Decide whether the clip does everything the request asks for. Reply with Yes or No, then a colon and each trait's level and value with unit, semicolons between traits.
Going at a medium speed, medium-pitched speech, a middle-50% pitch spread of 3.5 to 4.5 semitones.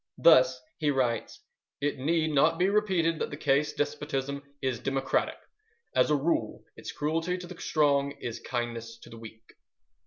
Yes: average, 160 wpm; medium, 145 Hz; average, 3.8 semitones